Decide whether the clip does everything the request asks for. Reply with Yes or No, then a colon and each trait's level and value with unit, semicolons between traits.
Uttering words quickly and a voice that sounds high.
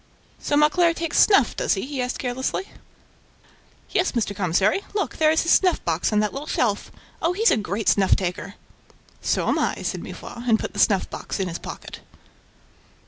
No: average, 190 wpm; high, 245 Hz